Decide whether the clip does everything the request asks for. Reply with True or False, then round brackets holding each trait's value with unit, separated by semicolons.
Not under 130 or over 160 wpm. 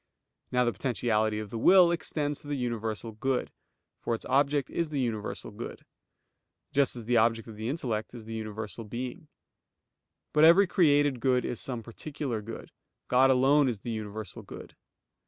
False (170 wpm)